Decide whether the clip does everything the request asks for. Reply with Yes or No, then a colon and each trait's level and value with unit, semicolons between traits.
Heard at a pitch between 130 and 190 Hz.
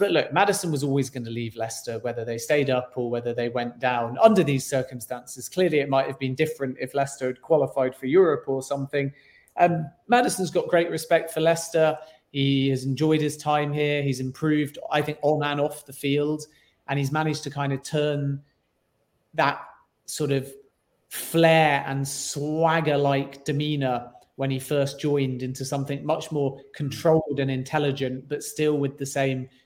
Yes: medium, 140 Hz